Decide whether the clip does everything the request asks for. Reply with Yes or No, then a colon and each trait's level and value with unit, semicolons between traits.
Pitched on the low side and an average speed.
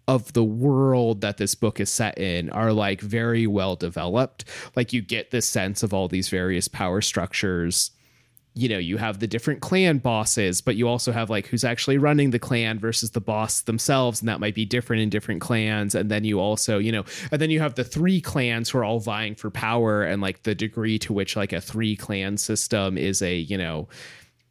No: low, 110 Hz; fast, 220 wpm